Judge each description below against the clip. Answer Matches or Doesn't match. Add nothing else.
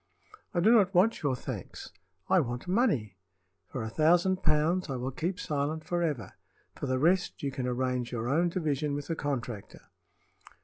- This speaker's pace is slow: Doesn't match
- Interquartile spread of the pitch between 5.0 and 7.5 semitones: Matches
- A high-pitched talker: Doesn't match